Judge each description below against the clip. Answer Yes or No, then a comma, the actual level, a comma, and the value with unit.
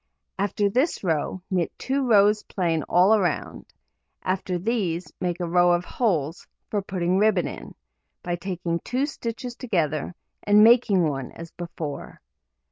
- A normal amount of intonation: Yes, average, 3.7 semitones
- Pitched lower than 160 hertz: No, medium, 185 Hz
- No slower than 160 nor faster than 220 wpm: No, average, 140 wpm